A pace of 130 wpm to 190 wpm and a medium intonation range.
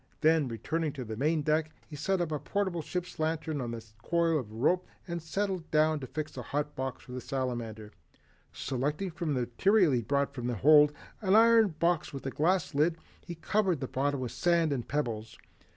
No: average, 200 wpm; average, 4.5 semitones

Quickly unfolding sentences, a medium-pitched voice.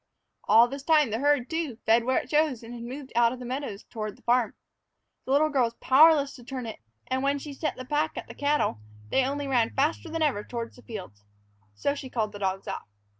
No: fast, 235 wpm; very high, 260 Hz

